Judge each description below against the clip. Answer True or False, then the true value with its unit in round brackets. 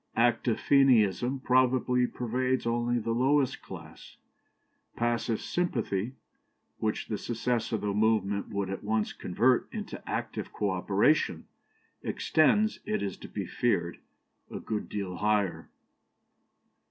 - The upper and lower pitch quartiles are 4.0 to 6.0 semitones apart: False (3.5 semitones)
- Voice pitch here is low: True (115 Hz)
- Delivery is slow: True (120 wpm)